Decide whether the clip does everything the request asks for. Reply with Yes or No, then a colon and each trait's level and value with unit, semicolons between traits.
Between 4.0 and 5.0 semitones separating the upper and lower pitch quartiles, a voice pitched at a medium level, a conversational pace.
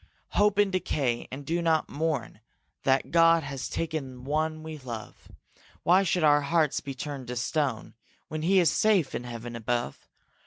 Yes: average, 4.3 semitones; medium, 150 Hz; average, 165 wpm